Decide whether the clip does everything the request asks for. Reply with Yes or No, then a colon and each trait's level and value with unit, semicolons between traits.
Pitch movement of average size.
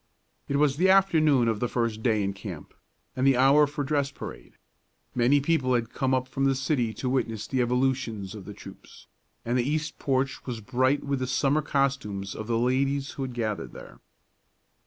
Yes: average, 3.1 semitones